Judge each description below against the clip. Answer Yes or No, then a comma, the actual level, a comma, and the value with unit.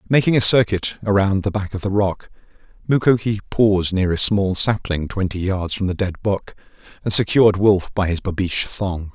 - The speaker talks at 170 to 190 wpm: Yes, average, 185 wpm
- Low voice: Yes, low, 100 Hz